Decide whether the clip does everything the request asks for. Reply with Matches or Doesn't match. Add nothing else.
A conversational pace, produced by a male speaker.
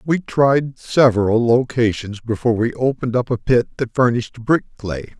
Matches